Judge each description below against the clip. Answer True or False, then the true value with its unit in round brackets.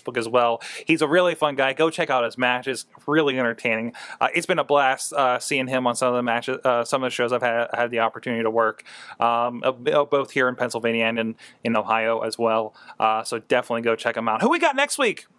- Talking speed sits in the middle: False (240 wpm)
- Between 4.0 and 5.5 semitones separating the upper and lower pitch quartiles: False (3.0 semitones)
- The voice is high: False (125 Hz)